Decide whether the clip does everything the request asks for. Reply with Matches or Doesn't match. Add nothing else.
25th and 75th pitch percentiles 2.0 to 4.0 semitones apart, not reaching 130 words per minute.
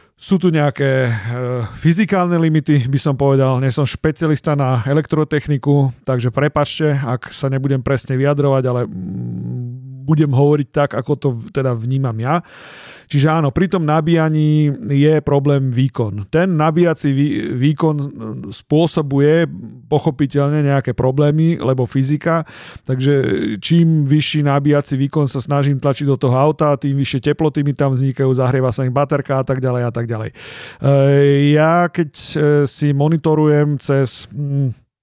Doesn't match